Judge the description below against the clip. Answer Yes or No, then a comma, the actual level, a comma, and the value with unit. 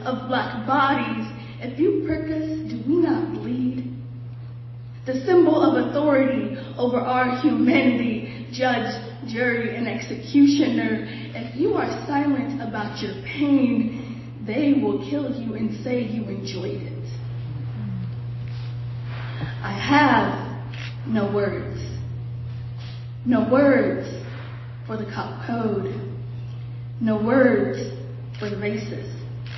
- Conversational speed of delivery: No, slow, 110 wpm